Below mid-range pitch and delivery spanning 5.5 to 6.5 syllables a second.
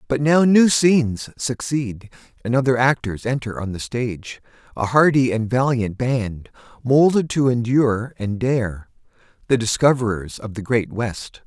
No: low, 120 Hz; 4.4 syllables/s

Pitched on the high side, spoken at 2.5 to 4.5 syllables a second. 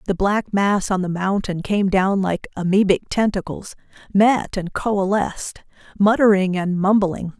Yes: high, 195 Hz; 4.4 syllables/s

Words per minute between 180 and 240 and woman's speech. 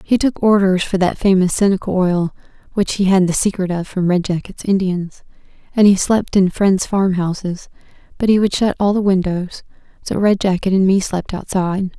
Yes: average, 190 wpm; female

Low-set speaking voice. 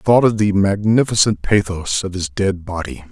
Yes: low, 100 Hz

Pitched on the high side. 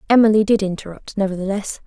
Yes: high, 200 Hz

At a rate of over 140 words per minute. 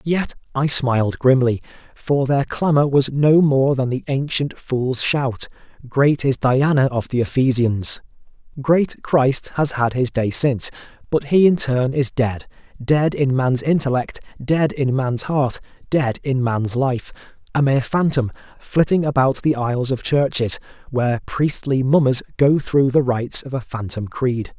Yes: average, 160 wpm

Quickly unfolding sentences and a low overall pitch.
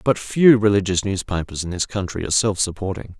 No: average, 190 wpm; low, 100 Hz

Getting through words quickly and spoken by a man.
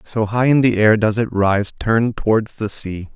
Yes: fast, 230 wpm; male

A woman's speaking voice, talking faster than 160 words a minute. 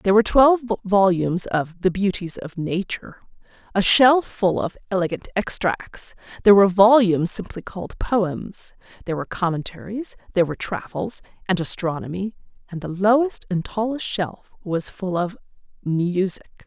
No: female; average, 140 wpm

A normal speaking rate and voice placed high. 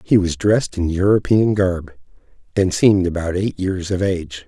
No: average, 175 wpm; very low, 95 Hz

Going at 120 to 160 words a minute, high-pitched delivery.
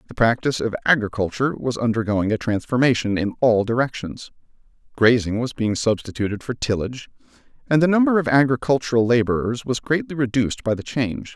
No: average, 155 wpm; low, 120 Hz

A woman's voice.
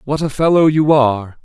No: male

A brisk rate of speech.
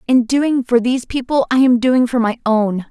Yes: fast, 225 wpm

